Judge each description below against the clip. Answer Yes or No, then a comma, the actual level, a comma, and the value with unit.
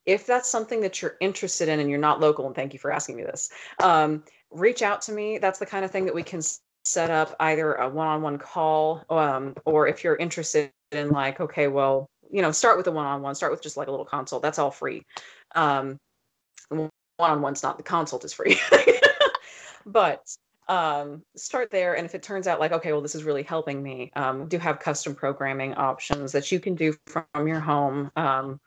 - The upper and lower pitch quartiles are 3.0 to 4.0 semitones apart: Yes, average, 3.6 semitones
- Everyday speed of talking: No, fast, 220 wpm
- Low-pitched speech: No, medium, 155 Hz